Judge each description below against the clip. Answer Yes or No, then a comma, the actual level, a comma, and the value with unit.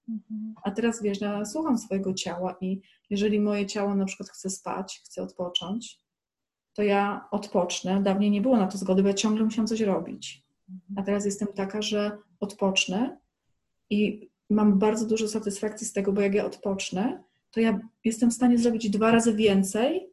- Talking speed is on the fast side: Yes, fast, 175 wpm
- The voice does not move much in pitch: Yes, narrow, 2.0 semitones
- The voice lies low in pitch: No, high, 205 Hz